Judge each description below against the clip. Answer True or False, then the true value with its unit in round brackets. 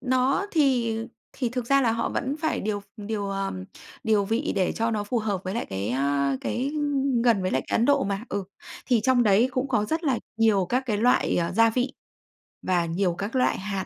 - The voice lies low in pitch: False (225 Hz)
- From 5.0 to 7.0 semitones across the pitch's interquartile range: False (4.5 semitones)